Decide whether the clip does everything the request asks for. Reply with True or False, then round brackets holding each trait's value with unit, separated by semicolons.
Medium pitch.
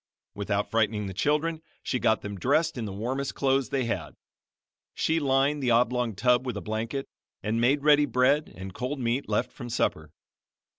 False (125 Hz)